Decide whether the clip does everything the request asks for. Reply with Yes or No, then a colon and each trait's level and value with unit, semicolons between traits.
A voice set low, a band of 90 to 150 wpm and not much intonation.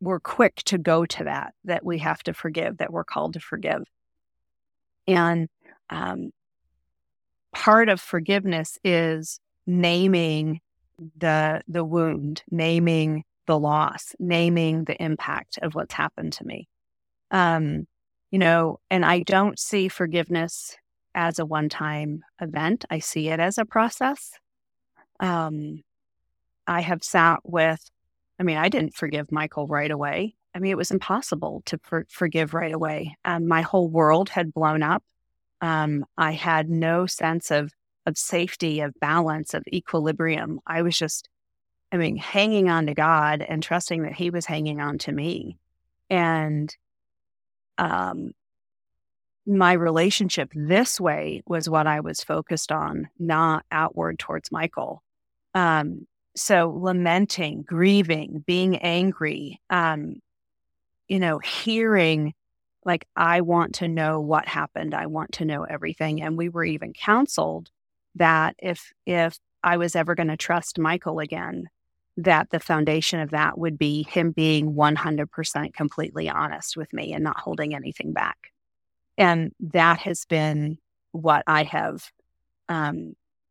No: medium, 165 Hz; average, 140 wpm; narrow, 2.2 semitones